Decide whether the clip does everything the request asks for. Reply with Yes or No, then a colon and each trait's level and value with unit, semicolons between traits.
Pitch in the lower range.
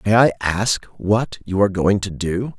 Yes: low, 100 Hz